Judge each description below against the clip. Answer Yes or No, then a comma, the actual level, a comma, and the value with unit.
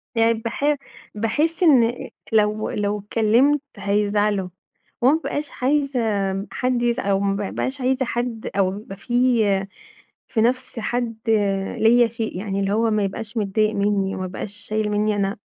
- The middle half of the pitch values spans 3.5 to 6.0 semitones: No, average, 3.1 semitones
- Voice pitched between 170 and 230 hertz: Yes, high, 220 Hz